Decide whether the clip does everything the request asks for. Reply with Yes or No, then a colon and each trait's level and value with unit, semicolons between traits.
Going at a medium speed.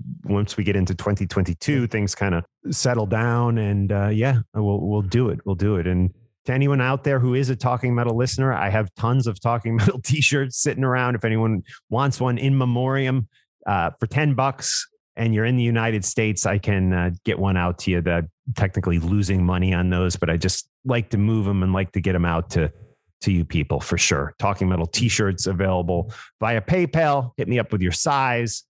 No: fast, 210 wpm